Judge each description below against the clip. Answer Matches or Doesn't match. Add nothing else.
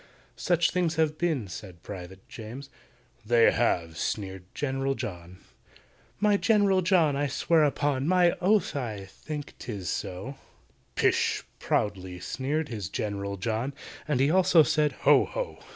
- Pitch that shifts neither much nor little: Doesn't match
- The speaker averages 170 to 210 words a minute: Doesn't match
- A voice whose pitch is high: Doesn't match